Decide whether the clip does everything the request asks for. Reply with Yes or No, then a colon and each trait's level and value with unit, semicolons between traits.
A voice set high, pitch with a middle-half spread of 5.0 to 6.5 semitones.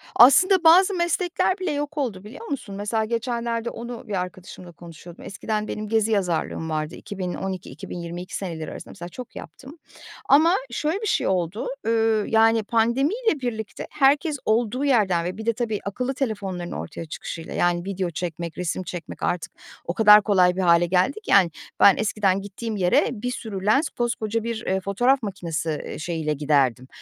Yes: high, 210 Hz; average, 5.3 semitones